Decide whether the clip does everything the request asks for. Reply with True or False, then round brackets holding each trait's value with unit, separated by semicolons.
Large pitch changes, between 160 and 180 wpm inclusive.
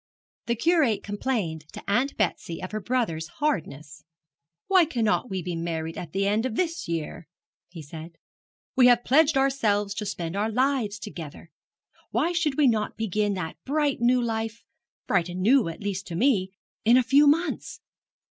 True (6.7 semitones; 170 wpm)